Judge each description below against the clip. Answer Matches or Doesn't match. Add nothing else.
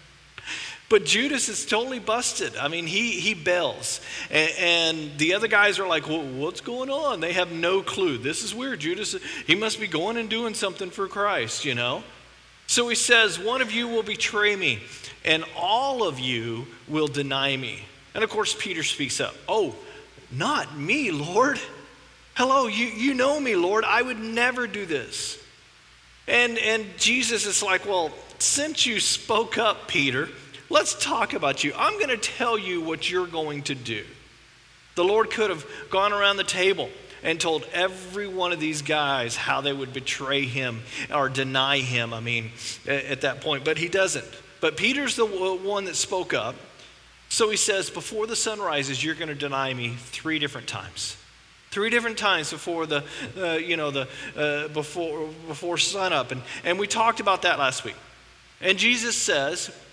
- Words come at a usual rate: Matches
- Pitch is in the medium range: Matches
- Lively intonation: Matches